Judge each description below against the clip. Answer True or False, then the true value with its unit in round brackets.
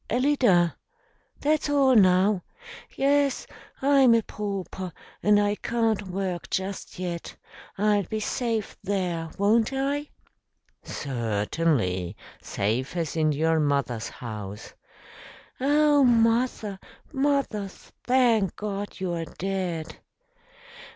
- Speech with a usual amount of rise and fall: False (6.4 semitones)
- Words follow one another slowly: True (100 wpm)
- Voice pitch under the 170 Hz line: False (200 Hz)